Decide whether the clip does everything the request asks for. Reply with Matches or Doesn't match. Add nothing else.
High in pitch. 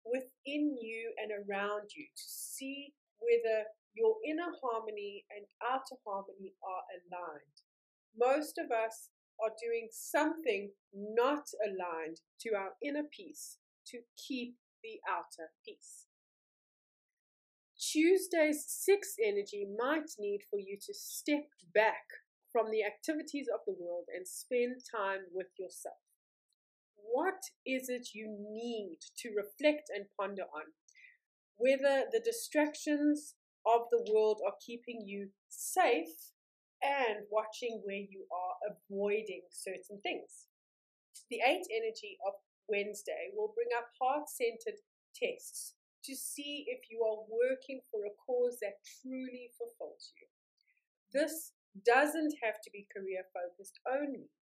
Matches